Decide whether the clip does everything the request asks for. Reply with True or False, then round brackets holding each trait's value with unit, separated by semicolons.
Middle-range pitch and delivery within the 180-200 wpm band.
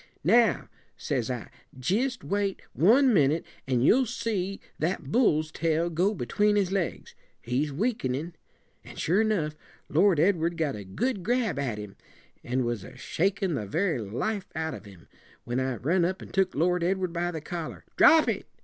False (170 Hz; 170 wpm)